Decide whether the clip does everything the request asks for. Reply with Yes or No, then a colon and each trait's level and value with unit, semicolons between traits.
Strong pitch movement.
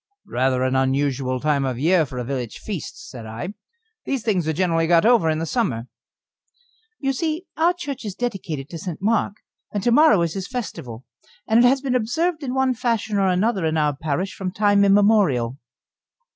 Yes: wide, 8.9 semitones